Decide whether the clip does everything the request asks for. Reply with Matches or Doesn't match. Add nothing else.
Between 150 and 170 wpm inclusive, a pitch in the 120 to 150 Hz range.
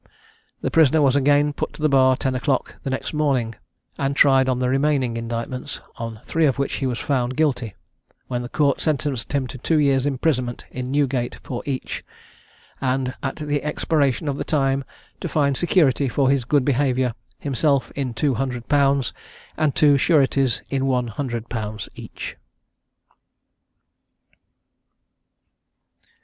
Matches